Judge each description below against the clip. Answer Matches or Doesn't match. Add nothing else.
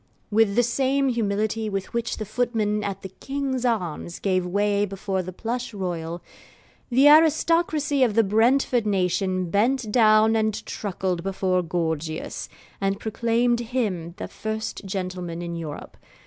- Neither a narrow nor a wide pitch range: Matches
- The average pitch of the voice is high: Matches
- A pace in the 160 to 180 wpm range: Doesn't match